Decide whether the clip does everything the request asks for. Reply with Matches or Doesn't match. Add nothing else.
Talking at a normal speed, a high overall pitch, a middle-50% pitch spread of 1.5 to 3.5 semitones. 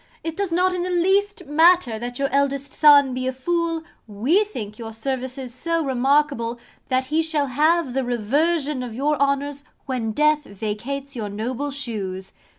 Doesn't match